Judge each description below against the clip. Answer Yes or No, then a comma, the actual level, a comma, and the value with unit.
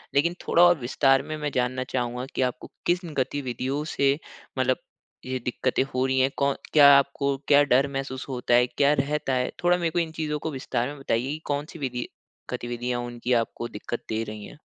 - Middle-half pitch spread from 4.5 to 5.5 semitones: No, average, 2.8 semitones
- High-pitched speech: No, low, 135 Hz